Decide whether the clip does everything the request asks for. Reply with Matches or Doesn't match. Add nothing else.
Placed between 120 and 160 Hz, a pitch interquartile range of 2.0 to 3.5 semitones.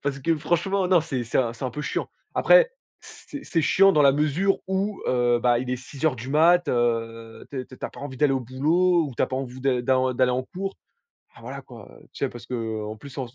Doesn't match